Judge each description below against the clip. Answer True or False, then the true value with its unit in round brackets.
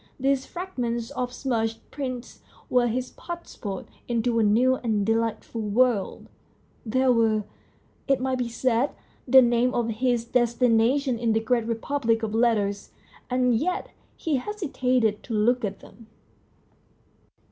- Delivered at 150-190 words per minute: False (135 wpm)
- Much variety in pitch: False (2.4 semitones)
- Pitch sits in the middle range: False (240 Hz)